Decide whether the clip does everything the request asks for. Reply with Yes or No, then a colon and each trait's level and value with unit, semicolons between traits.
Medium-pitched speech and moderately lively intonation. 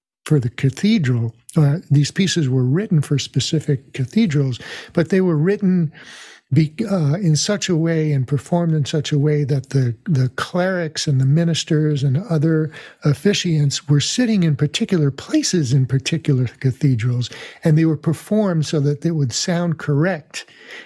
Yes: medium, 155 Hz; average, 3.6 semitones